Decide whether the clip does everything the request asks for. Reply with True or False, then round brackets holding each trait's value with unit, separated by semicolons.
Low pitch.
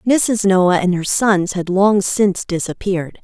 False (190 Hz)